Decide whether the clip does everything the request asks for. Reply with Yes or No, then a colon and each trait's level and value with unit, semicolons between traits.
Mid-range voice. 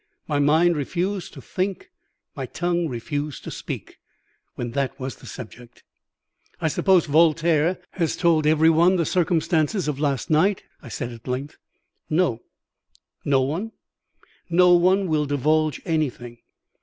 Yes: medium, 155 Hz